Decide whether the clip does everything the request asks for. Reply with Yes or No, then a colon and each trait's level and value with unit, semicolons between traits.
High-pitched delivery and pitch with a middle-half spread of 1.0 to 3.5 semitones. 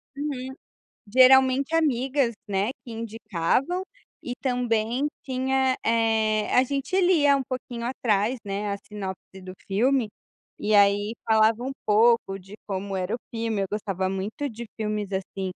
No: high, 225 Hz; average, 4.2 semitones